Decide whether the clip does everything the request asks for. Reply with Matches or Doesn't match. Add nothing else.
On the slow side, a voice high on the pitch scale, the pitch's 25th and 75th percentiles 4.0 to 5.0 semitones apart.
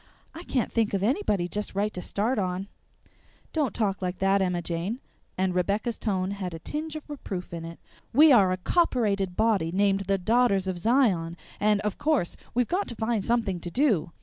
Doesn't match